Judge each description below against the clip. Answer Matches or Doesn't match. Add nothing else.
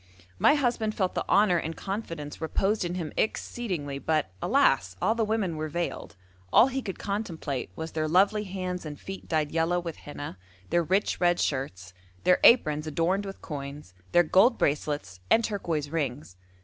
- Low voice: Doesn't match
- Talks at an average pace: Matches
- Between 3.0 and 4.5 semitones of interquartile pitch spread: Doesn't match